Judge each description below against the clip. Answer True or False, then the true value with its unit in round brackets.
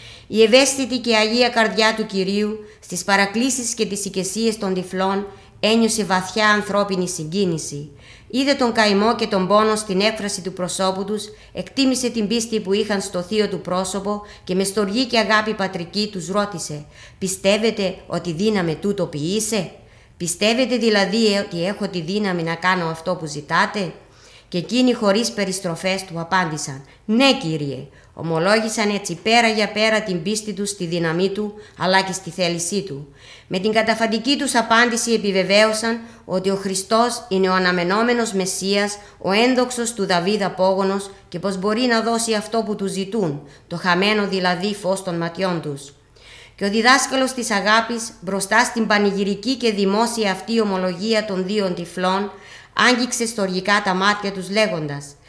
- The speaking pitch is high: True (200 Hz)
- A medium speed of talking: True (155 wpm)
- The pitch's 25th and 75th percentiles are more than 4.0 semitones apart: False (3.1 semitones)